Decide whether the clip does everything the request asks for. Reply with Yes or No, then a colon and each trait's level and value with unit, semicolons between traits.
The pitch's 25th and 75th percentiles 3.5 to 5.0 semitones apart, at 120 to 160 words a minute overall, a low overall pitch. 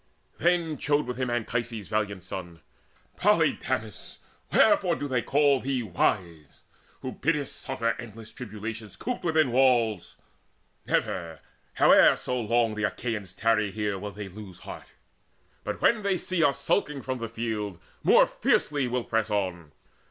Yes: average, 4.4 semitones; average, 145 wpm; low, 115 Hz